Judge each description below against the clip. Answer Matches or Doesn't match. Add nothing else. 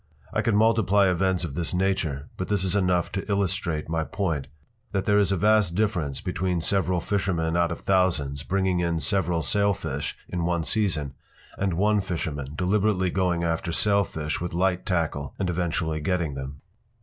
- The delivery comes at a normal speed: Matches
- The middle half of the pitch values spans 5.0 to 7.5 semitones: Doesn't match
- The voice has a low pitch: Matches